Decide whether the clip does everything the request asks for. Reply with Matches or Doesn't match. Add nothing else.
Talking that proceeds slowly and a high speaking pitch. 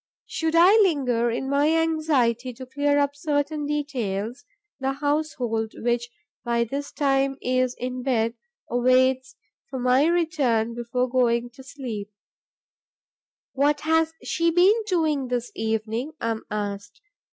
Matches